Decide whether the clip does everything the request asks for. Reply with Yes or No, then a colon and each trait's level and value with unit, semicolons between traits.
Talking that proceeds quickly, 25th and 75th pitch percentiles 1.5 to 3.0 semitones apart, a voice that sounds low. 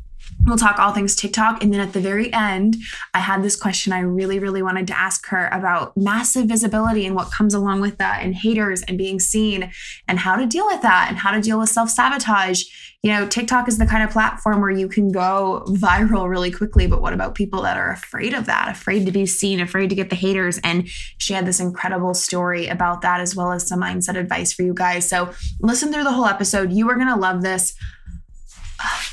No: fast, 230 wpm; narrow, 2.6 semitones; high, 195 Hz